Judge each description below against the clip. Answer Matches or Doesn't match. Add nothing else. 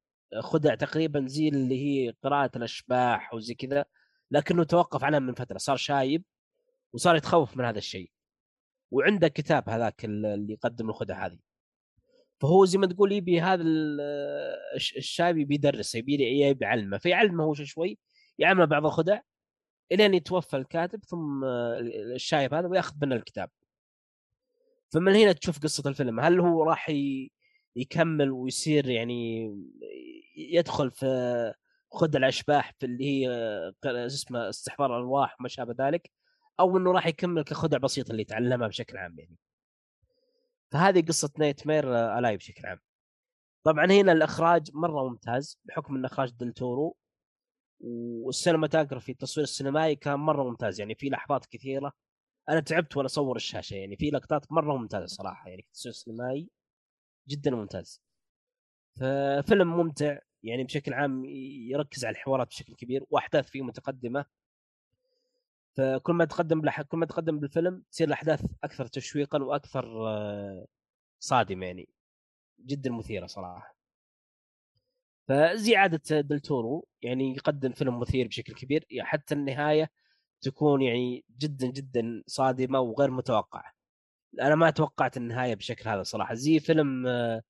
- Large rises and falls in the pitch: Doesn't match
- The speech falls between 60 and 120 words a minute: Doesn't match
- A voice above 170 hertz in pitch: Doesn't match